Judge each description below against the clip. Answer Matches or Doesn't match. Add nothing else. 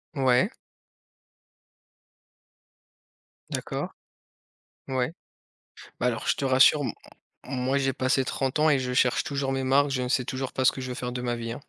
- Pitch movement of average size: Doesn't match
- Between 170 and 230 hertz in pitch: Doesn't match